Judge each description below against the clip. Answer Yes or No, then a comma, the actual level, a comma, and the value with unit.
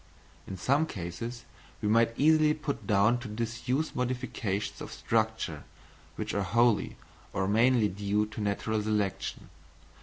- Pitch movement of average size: Yes, average, 3.4 semitones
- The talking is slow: Yes, slow, 130 wpm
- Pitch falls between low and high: No, low, 115 Hz